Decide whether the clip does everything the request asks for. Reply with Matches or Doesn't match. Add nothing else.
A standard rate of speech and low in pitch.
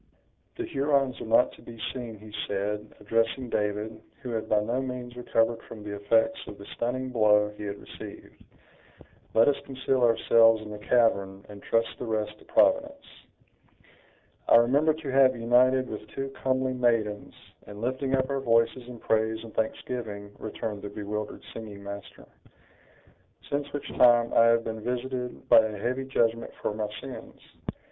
Matches